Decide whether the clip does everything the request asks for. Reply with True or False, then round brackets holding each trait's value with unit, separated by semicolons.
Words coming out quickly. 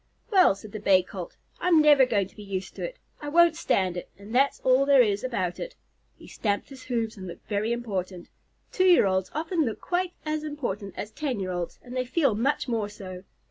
True (220 wpm)